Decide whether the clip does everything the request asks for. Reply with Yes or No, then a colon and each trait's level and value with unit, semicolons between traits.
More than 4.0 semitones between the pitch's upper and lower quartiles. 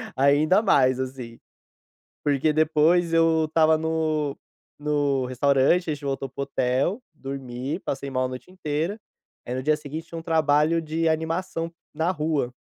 No: average, 3.0 semitones